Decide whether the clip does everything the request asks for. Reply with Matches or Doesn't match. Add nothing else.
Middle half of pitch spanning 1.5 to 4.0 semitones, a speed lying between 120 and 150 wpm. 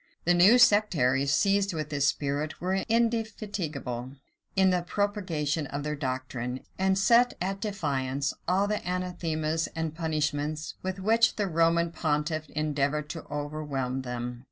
Doesn't match